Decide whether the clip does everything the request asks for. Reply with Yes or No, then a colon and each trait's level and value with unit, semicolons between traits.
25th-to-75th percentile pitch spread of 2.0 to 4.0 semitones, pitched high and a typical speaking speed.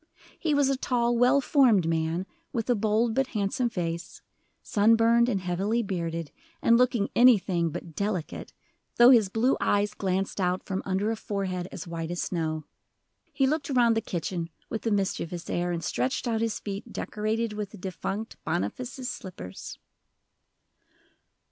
No: average, 5.0 semitones; high, 205 Hz; average, 160 wpm